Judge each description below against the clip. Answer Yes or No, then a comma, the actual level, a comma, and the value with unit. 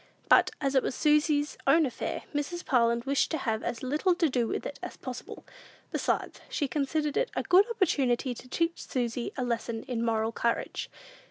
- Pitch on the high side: Yes, very high, 270 Hz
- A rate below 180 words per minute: No, average, 185 wpm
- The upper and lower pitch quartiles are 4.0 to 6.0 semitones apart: Yes, average, 4.4 semitones